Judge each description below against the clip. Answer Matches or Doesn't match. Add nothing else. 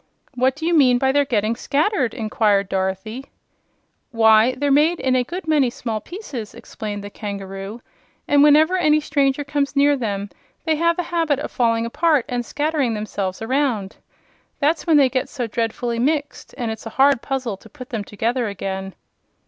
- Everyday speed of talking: Matches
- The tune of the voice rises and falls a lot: Doesn't match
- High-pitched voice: Matches